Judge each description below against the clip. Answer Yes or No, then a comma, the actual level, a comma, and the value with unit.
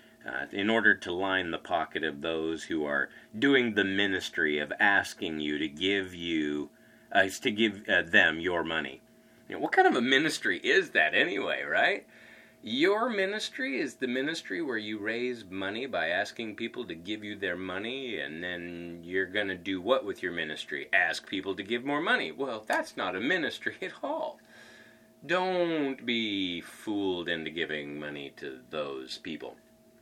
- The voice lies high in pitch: No, low, 105 Hz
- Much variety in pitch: Yes, wide, 7.6 semitones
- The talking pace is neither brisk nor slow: Yes, average, 175 wpm